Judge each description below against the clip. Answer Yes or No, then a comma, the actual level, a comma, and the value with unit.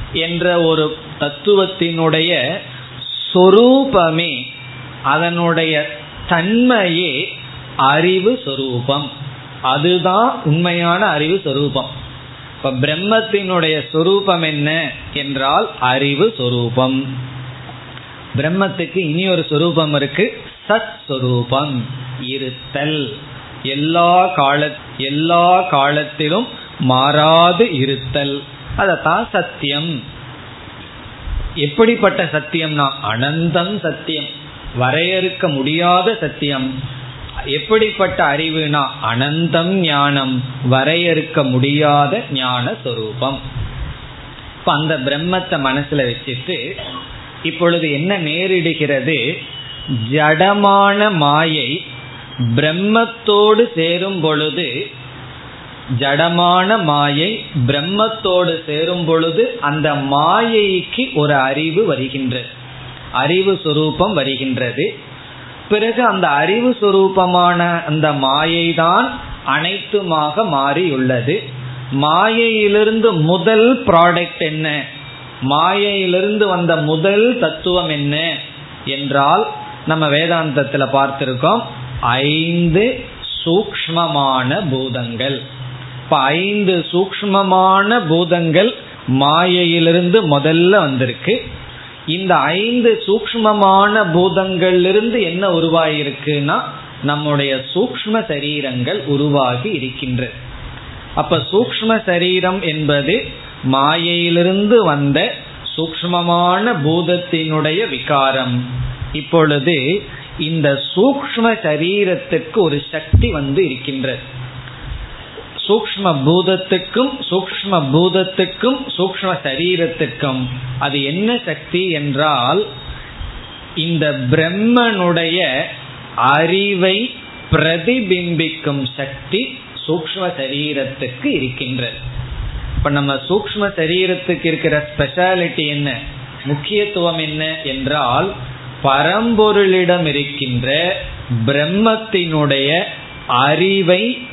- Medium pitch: Yes, medium, 155 Hz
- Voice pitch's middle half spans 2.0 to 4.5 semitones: No, average, 5.0 semitones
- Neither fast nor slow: No, slow, 65 wpm